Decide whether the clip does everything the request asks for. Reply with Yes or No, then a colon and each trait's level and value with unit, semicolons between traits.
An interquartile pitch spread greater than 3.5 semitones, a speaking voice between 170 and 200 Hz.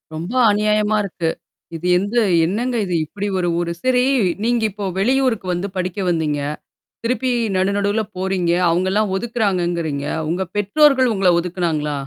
Yes: average, 4.1 semitones; high, 195 Hz